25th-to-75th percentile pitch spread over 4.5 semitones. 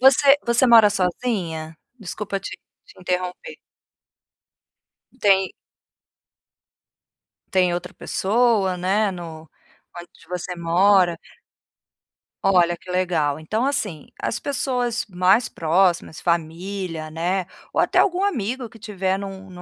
No: average, 3.9 semitones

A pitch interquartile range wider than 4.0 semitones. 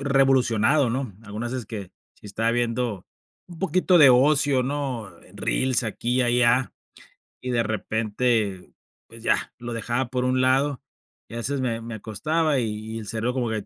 No: average, 2.7 semitones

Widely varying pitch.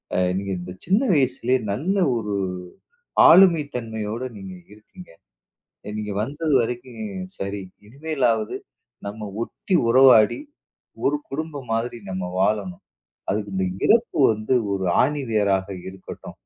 Yes: wide, 6.0 semitones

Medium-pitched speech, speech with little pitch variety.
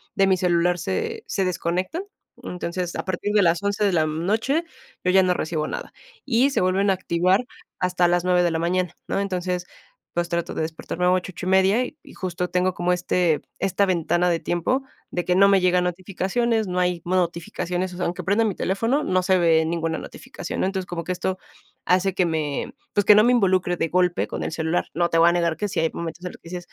Yes: medium, 180 Hz; narrow, 1.9 semitones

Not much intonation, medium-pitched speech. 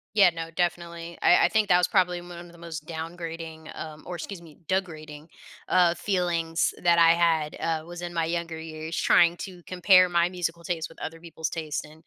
Yes: narrow, 1.4 semitones; medium, 170 Hz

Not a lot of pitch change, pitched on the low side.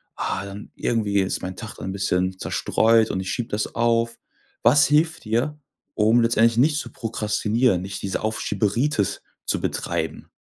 No: average, 3.2 semitones; low, 110 Hz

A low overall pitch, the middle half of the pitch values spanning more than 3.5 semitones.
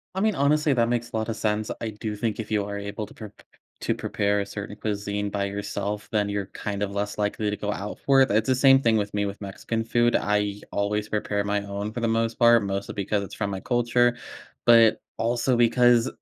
No: low, 105 Hz; narrow, 2.5 semitones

